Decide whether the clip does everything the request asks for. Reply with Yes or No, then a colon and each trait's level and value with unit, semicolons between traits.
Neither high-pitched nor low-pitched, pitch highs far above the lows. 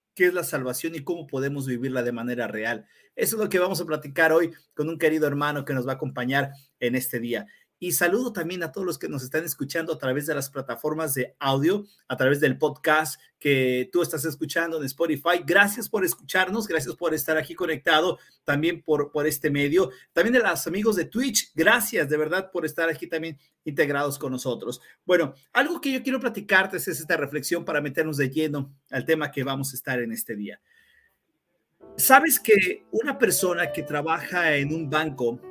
No: medium, 160 Hz; average, 4.1 semitones